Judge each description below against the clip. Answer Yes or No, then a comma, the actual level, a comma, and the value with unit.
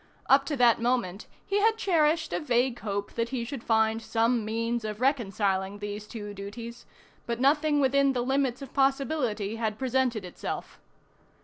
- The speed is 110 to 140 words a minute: No, average, 165 wpm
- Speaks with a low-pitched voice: No, high, 240 Hz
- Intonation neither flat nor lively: Yes, average, 4.0 semitones